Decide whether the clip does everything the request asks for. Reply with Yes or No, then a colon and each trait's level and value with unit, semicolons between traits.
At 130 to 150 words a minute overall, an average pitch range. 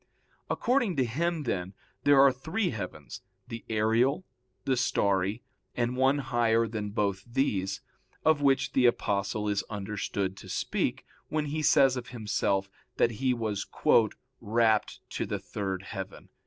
Yes: average, 140 wpm; average, 4.7 semitones